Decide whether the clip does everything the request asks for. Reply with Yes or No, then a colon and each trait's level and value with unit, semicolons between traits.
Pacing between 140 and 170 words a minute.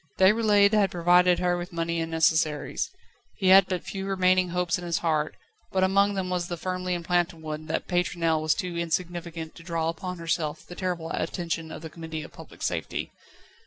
No: average, 190 wpm